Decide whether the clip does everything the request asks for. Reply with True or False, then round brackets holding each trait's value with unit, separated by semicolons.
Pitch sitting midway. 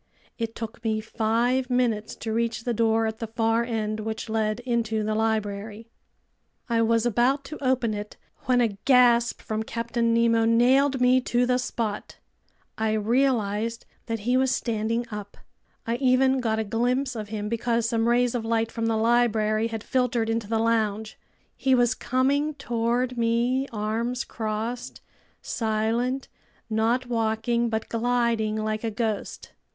False (230 Hz)